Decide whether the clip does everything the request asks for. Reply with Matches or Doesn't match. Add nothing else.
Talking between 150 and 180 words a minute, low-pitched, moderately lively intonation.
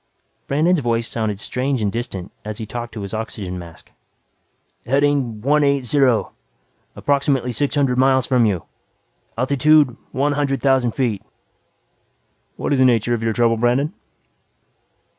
Doesn't match